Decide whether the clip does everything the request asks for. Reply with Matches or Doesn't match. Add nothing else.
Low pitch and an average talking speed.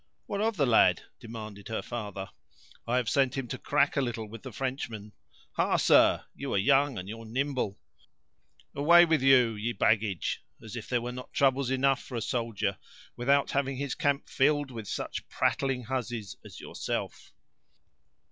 Matches